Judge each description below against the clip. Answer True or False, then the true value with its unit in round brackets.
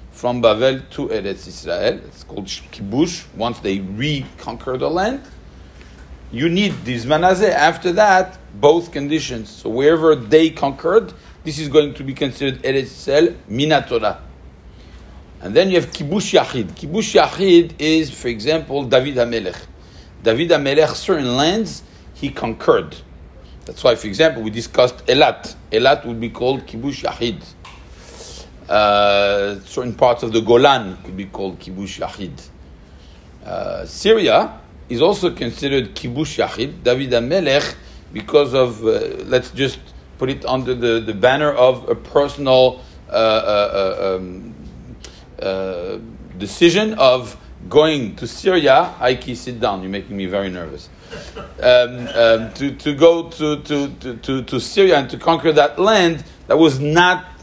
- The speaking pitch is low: True (125 Hz)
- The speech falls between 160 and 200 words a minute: False (140 wpm)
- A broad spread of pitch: True (7.3 semitones)